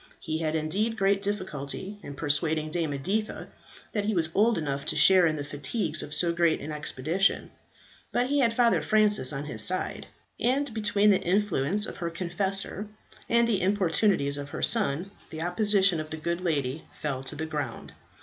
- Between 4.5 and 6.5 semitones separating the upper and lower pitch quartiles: Yes, average, 5.2 semitones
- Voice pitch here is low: No, medium, 175 Hz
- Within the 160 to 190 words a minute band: Yes, average, 180 wpm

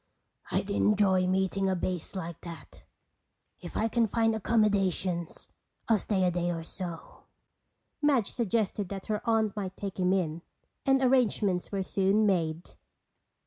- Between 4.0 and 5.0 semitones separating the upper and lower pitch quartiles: No, average, 3.1 semitones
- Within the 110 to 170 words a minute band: Yes, average, 145 wpm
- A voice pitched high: Yes, high, 195 Hz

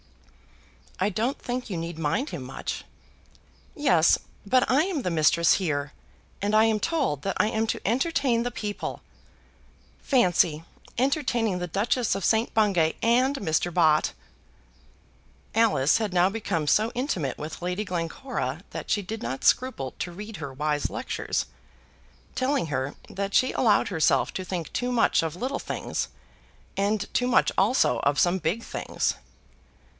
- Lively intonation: Yes, wide, 6.8 semitones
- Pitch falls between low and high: No, high, 200 Hz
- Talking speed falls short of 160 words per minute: Yes, average, 150 wpm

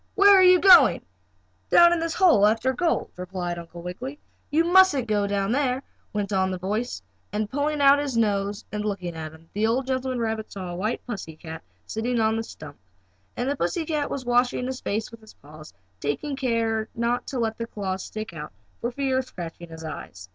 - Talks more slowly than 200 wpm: No, fast, 205 wpm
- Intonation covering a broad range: Yes, wide, 5.9 semitones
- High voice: Yes, high, 225 Hz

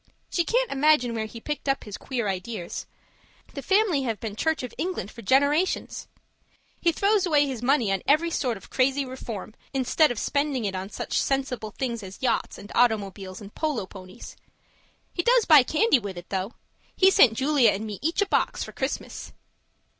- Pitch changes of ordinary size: No, wide, 6.3 semitones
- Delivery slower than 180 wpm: No, average, 185 wpm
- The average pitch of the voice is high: Yes, very high, 255 Hz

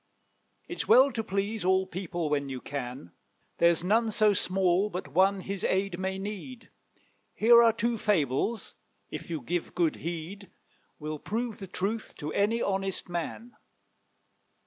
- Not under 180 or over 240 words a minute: No, average, 145 wpm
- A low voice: No, high, 190 Hz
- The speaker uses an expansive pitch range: No, average, 4.0 semitones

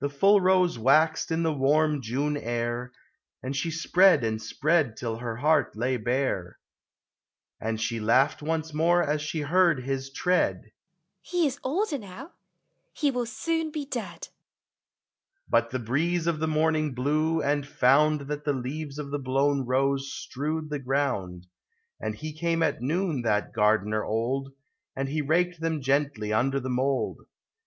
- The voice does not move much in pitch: No, average, 4.2 semitones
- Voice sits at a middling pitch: Yes, medium, 145 Hz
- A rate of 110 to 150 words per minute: No, average, 165 wpm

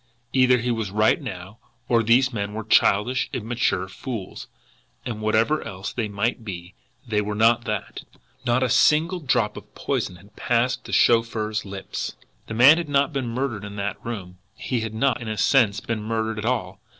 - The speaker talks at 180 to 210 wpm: Yes, average, 185 wpm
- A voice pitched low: Yes, low, 115 Hz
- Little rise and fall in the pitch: No, average, 3.2 semitones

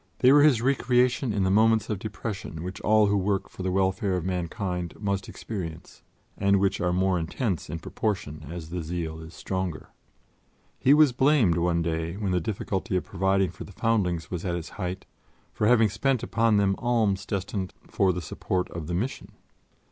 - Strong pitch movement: No, average, 3.6 semitones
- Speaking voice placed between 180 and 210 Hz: No, very low, 95 Hz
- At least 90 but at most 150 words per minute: No, average, 185 wpm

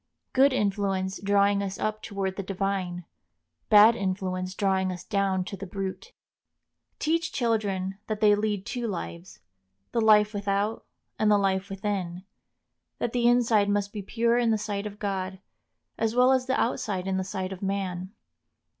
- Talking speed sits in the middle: Yes, average, 165 wpm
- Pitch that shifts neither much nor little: No, narrow, 2.2 semitones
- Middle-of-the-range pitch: No, high, 200 Hz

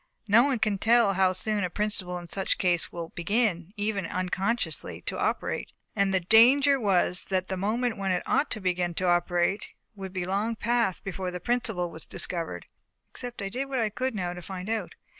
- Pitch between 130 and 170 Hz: No, high, 195 Hz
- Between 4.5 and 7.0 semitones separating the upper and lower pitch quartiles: No, average, 3.8 semitones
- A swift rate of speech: Yes, fast, 210 wpm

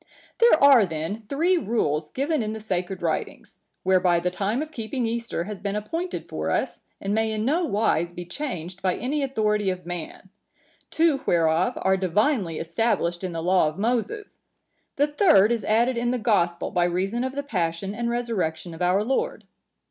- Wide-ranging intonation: Yes, wide, 5.9 semitones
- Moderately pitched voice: No, high, 210 Hz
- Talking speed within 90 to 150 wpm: No, average, 180 wpm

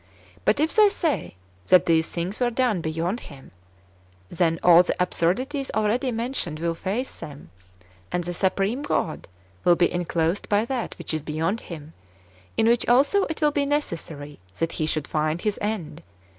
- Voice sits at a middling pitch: Yes, medium, 180 Hz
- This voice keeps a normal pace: Yes, average, 170 wpm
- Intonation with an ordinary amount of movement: No, wide, 7.0 semitones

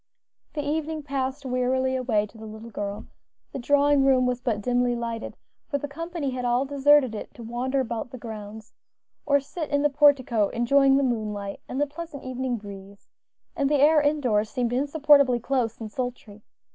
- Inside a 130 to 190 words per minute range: Yes, average, 180 wpm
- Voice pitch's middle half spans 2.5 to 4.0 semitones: Yes, average, 3.7 semitones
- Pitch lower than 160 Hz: No, very high, 255 Hz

